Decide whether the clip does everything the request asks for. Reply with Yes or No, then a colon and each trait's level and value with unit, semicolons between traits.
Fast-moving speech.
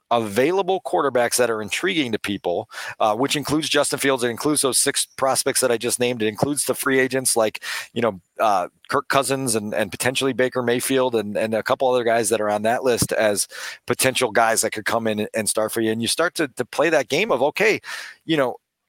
Yes: fast, 225 wpm